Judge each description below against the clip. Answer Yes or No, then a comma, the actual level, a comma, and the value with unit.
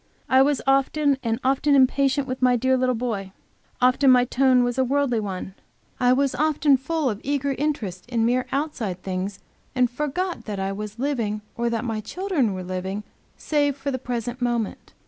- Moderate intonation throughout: Yes, average, 3.7 semitones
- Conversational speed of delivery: Yes, average, 180 wpm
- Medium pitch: No, very high, 255 Hz